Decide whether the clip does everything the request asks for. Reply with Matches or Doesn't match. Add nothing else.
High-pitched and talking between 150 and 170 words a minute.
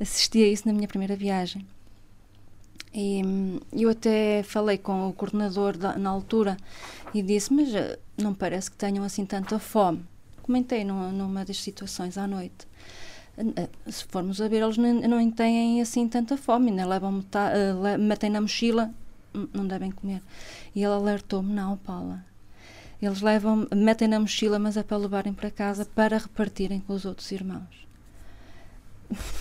Matches